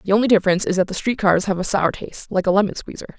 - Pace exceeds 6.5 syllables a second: Yes, 7.3 syllables/s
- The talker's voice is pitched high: Yes, high, 195 Hz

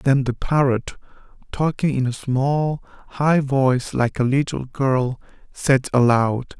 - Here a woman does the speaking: No, male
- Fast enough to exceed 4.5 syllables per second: No, 3.9 syllables/s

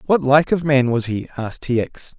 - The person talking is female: No, male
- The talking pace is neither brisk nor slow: No, fast, 245 wpm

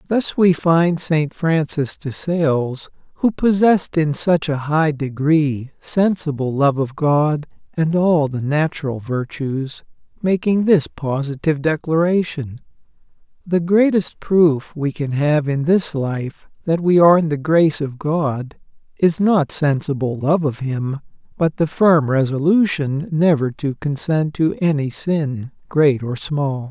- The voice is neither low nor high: Yes, medium, 155 Hz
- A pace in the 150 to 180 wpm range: No, average, 140 wpm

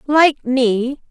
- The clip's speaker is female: Yes, female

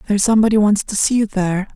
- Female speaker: No, male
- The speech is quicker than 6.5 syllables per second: Yes, 7.8 syllables/s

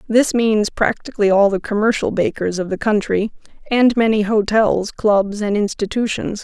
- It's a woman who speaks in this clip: Yes, female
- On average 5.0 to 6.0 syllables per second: No, 4.7 syllables/s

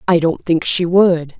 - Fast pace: Yes, fast, 215 wpm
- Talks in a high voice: No, medium, 170 Hz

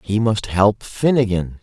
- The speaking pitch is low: Yes, low, 105 Hz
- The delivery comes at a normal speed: Yes, average, 150 wpm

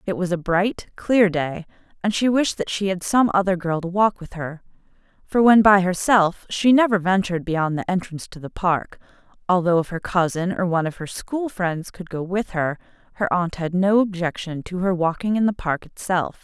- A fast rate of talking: Yes, fast, 210 wpm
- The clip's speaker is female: Yes, female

